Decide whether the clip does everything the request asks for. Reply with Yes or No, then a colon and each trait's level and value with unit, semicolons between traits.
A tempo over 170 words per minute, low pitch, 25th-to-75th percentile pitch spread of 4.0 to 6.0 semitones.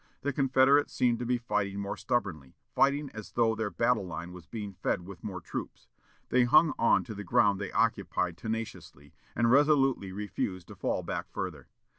Yes: average, 180 wpm; low, 110 Hz; average, 4.8 semitones